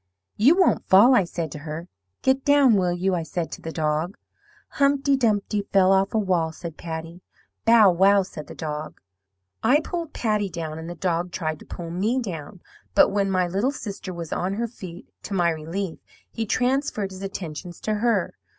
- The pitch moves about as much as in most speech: Yes, average, 4.6 semitones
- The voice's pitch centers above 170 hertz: Yes, high, 190 Hz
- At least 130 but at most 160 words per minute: No, average, 190 wpm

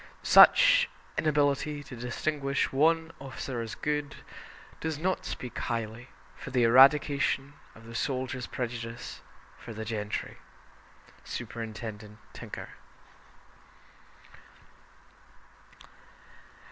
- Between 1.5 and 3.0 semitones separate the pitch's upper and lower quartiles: No, average, 4.3 semitones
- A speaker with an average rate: No, slow, 85 wpm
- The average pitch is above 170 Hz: No, low, 130 Hz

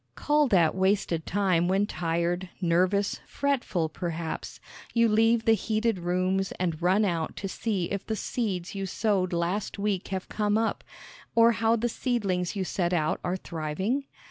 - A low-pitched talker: No, high, 190 Hz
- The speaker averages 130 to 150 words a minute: No, average, 160 wpm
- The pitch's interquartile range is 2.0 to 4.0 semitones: Yes, average, 3.7 semitones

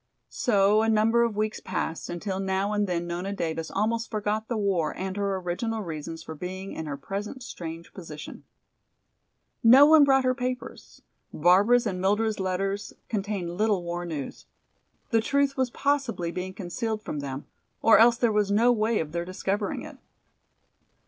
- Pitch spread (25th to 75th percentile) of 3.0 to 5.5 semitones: Yes, average, 4.3 semitones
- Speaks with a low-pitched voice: No, high, 200 Hz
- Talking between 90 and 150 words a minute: No, average, 165 wpm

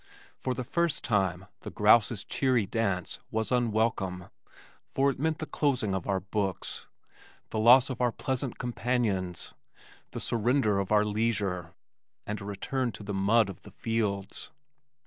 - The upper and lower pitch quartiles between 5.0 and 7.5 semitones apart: No, average, 3.9 semitones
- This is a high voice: No, low, 110 Hz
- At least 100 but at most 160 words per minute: Yes, average, 150 wpm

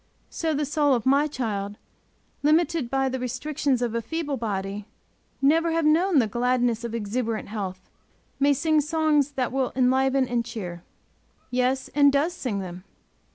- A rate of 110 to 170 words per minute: Yes, average, 155 wpm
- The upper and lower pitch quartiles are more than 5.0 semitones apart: No, average, 4.4 semitones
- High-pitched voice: Yes, very high, 260 Hz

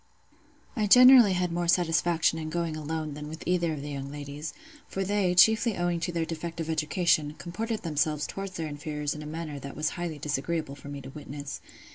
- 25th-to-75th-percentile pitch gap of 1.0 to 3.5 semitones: Yes, average, 2.9 semitones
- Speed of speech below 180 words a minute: No, average, 195 wpm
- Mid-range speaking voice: Yes, medium, 160 Hz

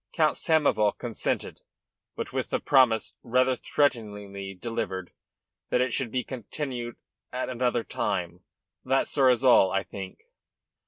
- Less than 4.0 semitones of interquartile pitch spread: No, average, 4.5 semitones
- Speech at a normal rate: No, slow, 130 wpm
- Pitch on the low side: Yes, low, 120 Hz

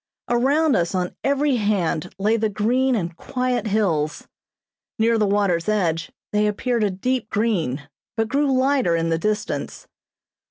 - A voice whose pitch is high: Yes, high, 215 Hz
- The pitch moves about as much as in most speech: No, wide, 5.8 semitones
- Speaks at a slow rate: No, average, 150 wpm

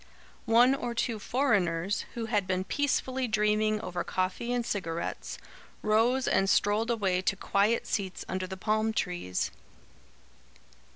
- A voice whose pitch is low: No, high, 210 Hz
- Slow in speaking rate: Yes, slow, 130 wpm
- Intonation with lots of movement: No, average, 3.8 semitones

